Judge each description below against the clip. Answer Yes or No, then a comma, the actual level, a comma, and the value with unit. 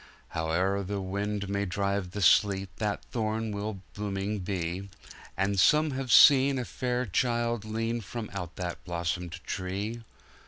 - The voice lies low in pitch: Yes, low, 100 Hz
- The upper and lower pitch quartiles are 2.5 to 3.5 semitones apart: Yes, average, 3.1 semitones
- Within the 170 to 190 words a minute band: No, average, 140 wpm